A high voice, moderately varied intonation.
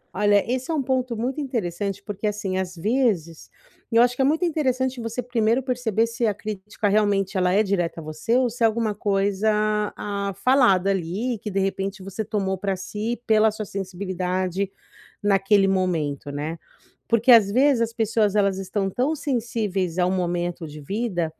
Yes: high, 205 Hz; average, 3.7 semitones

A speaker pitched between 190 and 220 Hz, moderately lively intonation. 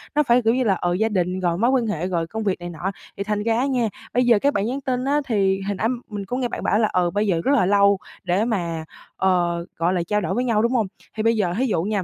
Yes: high, 210 Hz; average, 4.4 semitones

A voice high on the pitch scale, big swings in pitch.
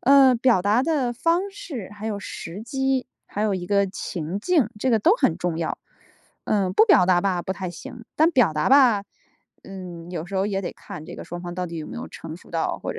Yes: high, 200 Hz; wide, 6.5 semitones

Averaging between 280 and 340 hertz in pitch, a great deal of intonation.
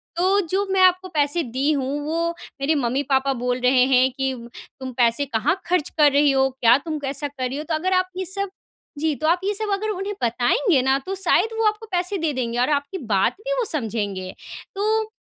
Yes: very high, 290 Hz; wide, 6.2 semitones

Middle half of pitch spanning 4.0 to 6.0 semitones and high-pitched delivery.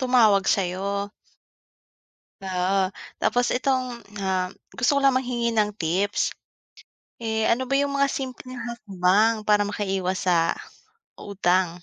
Yes: average, 4.6 semitones; high, 210 Hz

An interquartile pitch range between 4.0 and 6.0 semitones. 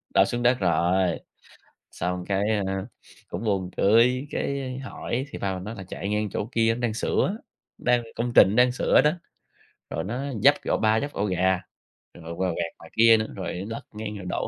Yes: average, 4.3 semitones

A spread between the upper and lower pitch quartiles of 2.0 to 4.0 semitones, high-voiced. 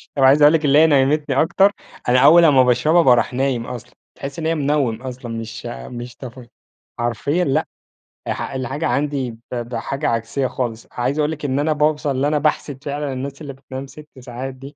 No: average, 3.0 semitones; low, 135 Hz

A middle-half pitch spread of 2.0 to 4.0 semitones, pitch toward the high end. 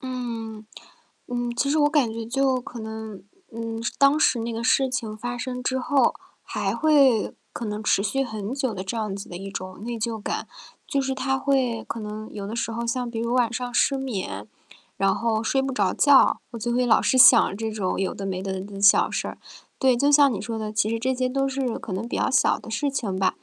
Yes: average, 3.4 semitones; high, 235 Hz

